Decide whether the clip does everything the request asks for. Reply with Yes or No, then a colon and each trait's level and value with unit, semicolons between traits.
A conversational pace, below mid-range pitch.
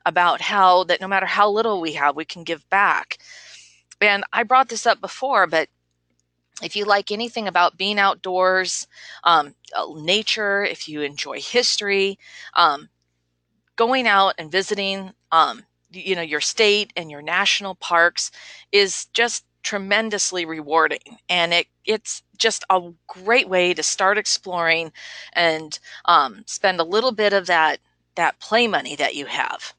No: average, 150 wpm; high, 190 Hz